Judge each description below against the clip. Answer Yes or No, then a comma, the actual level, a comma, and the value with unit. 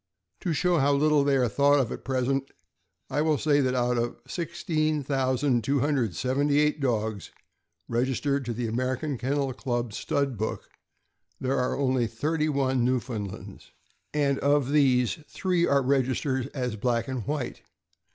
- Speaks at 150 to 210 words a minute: No, average, 140 wpm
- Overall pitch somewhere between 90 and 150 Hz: Yes, low, 135 Hz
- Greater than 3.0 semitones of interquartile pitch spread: No, average, 2.7 semitones